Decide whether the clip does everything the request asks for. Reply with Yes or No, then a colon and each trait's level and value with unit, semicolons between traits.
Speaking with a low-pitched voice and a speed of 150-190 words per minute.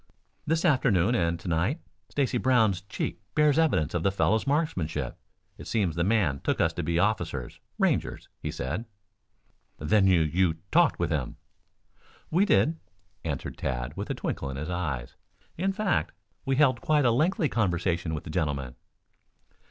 Yes: very low, 95 Hz; average, 160 wpm